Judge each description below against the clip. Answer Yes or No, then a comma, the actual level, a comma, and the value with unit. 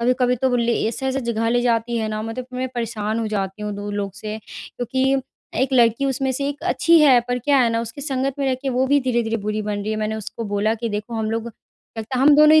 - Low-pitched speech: No, high, 235 Hz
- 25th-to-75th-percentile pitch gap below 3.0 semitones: No, average, 3.3 semitones